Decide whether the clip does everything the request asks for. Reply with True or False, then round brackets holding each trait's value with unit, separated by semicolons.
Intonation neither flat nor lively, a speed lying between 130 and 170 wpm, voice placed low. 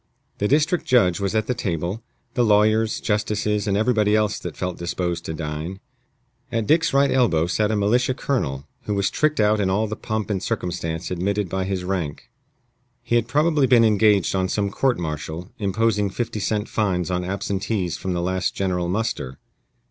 False (3.6 semitones; 180 wpm; 100 Hz)